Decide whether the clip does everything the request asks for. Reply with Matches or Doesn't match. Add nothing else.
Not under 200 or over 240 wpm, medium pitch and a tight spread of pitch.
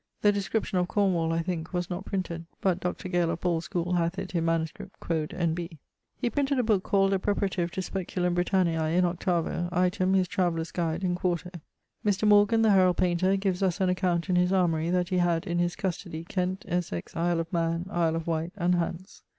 Matches